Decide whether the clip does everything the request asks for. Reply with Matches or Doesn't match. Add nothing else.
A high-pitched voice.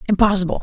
Matches